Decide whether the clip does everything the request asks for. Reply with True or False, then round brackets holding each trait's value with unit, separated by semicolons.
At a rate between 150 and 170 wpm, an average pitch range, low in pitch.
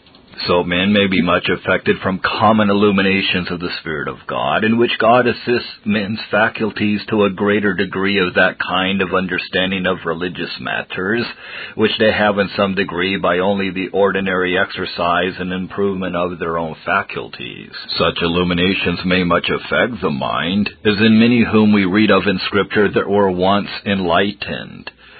False (165 wpm; 2.3 semitones; 95 Hz)